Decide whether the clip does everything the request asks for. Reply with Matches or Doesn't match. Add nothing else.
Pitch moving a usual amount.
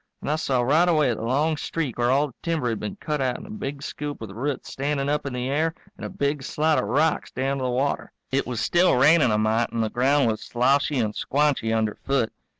Matches